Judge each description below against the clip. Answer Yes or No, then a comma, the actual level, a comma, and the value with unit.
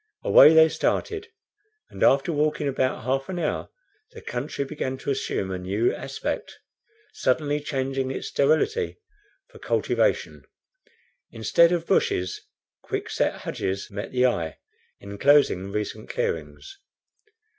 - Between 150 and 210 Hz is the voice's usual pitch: No, low, 135 Hz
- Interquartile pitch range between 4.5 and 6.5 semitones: Yes, average, 5.1 semitones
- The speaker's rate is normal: No, slow, 125 wpm